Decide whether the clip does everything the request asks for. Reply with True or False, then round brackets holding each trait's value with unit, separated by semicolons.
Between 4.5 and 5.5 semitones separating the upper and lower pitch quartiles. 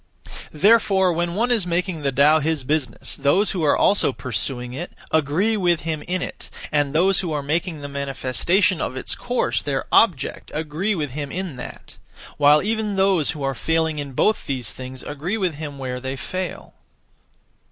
True (4.8 semitones)